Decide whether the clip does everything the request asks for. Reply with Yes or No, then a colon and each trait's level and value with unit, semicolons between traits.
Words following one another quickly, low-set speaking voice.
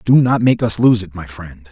Yes: fast, 280 wpm; low, 105 Hz